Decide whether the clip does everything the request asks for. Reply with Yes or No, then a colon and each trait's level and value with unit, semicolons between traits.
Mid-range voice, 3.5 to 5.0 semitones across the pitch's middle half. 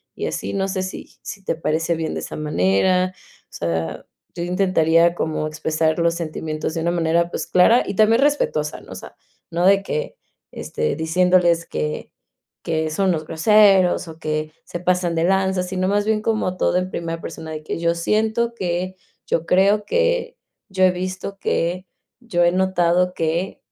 No: medium, 180 Hz; average, 2.9 semitones